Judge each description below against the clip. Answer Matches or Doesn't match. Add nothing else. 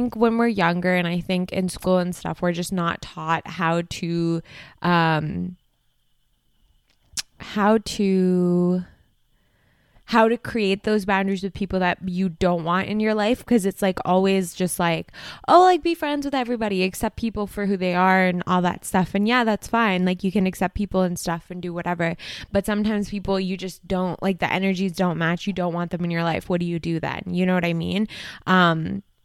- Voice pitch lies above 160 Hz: Matches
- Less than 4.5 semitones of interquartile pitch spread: Matches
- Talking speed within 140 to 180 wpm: Doesn't match